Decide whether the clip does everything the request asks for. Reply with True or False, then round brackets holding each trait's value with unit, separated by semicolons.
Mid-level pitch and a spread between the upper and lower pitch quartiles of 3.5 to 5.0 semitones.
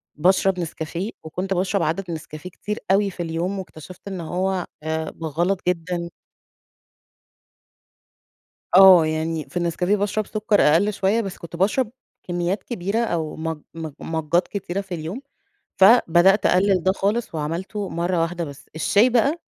False (180 Hz; 3.1 semitones)